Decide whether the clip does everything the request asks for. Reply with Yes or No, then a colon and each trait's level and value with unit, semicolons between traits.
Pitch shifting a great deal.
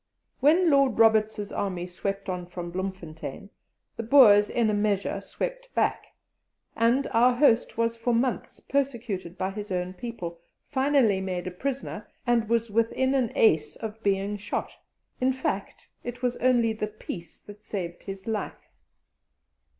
No: average, 4.2 semitones